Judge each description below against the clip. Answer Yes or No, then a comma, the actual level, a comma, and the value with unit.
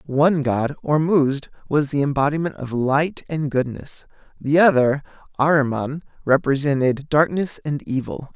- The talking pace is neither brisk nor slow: No, slow, 120 wpm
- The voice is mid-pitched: Yes, medium, 145 Hz